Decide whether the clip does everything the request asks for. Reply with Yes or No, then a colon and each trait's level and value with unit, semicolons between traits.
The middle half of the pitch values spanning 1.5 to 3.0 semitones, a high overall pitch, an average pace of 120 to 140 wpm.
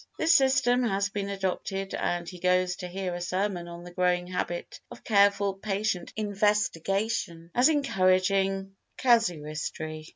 Yes: average, 2.7 semitones; high, 195 Hz; slow, 135 wpm